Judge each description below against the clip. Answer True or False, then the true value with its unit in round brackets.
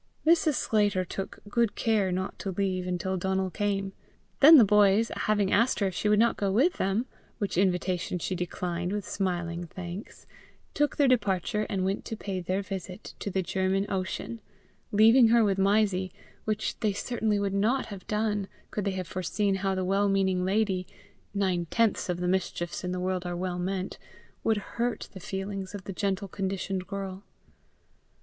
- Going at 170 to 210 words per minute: True (180 wpm)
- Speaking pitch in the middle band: False (195 Hz)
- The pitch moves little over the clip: True (2.1 semitones)